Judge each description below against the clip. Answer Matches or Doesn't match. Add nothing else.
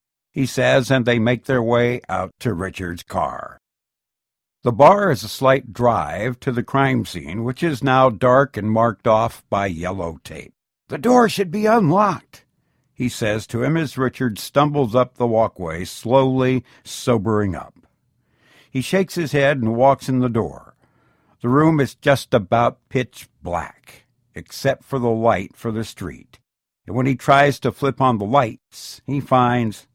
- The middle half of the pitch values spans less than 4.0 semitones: Matches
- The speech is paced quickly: Doesn't match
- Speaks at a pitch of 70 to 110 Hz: Doesn't match